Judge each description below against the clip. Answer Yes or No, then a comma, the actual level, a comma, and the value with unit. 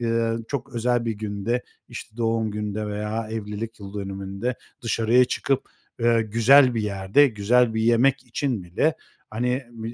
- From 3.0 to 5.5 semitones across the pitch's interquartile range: No, narrow, 2.6 semitones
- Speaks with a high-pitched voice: No, low, 115 Hz